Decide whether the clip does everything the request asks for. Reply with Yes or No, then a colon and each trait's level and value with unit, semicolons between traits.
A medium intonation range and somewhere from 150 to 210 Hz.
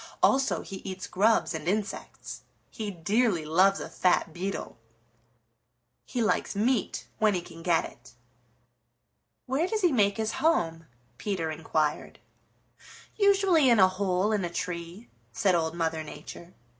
Yes: average, 4.8 semitones; high, 190 Hz